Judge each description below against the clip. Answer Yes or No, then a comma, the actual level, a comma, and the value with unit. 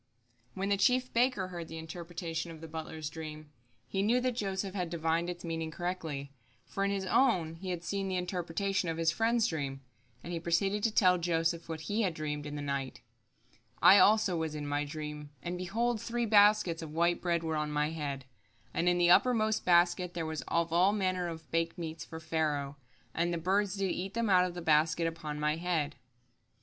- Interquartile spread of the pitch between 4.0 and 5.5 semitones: No, average, 3.3 semitones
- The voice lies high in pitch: No, medium, 170 Hz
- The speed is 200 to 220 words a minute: Yes, fast, 205 wpm